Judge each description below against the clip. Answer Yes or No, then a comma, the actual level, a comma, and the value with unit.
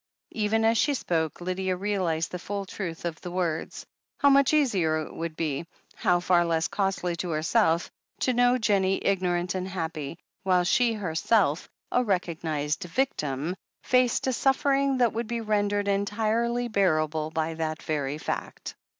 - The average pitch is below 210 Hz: Yes, medium, 185 Hz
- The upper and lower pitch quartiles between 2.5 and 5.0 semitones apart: No, wide, 5.4 semitones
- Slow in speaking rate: No, average, 155 wpm